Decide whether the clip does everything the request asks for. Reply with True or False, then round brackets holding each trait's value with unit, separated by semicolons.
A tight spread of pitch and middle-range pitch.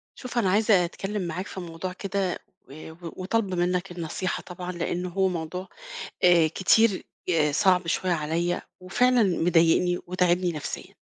True (1.9 semitones; 180 Hz)